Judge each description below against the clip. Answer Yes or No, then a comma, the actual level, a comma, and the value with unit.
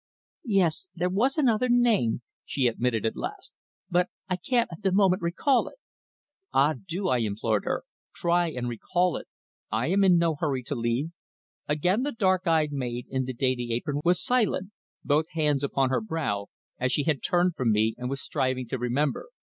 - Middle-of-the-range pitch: Yes, medium, 155 Hz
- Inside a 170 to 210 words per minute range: Yes, average, 185 wpm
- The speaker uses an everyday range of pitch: No, wide, 6.6 semitones